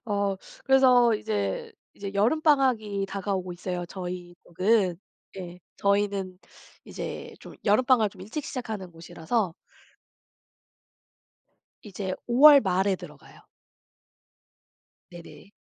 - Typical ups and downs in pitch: Yes, average, 3.8 semitones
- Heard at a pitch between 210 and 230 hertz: No, high, 200 Hz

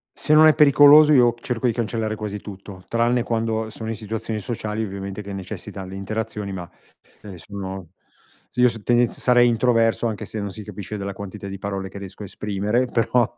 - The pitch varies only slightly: No, average, 3.1 semitones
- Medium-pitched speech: No, low, 110 Hz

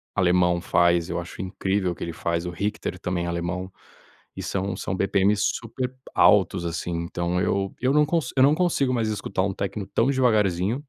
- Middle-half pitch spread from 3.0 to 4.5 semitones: Yes, average, 4.2 semitones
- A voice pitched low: Yes, very low, 95 Hz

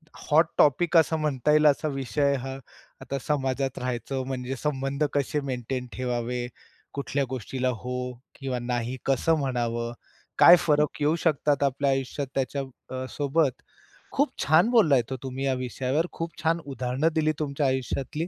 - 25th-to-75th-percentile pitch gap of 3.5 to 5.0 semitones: No, average, 2.8 semitones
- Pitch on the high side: No, low, 135 Hz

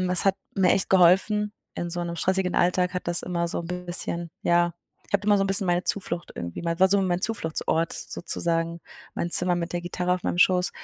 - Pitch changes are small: Yes, narrow, 1.6 semitones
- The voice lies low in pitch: No, medium, 180 Hz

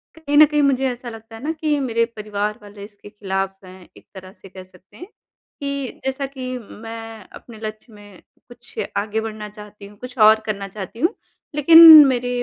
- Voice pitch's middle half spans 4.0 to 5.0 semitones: Yes, average, 4.4 semitones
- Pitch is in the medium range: No, high, 225 Hz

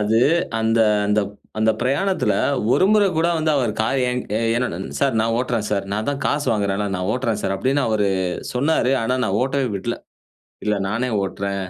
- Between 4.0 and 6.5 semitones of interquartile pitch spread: Yes, average, 4.5 semitones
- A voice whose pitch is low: Yes, low, 115 Hz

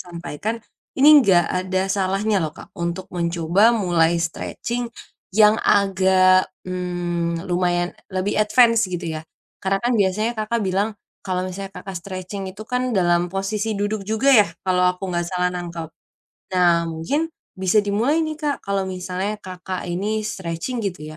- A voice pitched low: No, high, 190 Hz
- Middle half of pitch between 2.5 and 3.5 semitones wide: Yes, average, 3.2 semitones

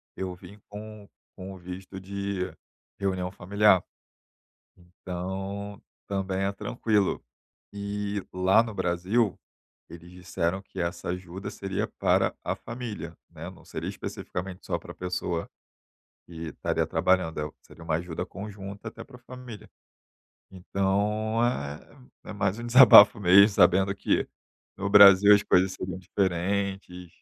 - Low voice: Yes, very low, 95 Hz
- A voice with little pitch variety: Yes, narrow, 2.1 semitones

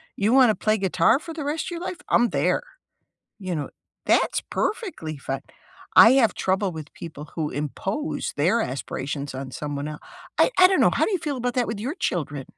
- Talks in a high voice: Yes, high, 195 Hz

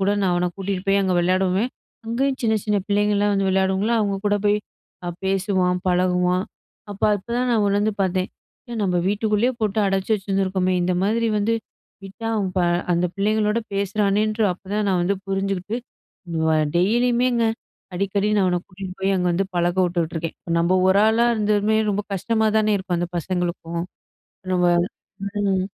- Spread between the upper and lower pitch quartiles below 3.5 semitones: Yes, narrow, 2.5 semitones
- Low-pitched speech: No, high, 195 Hz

